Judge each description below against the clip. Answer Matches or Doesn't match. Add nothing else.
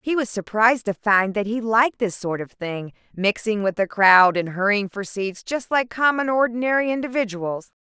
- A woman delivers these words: Matches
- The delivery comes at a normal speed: Matches